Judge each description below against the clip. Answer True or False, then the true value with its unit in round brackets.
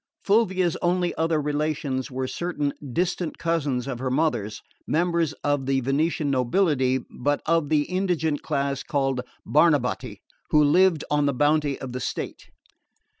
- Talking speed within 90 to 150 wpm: True (140 wpm)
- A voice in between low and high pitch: True (150 Hz)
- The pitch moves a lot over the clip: False (3.6 semitones)